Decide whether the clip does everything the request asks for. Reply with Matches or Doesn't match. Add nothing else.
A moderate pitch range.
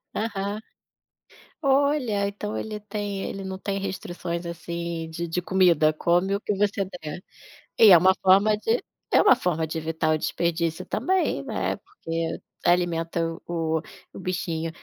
Matches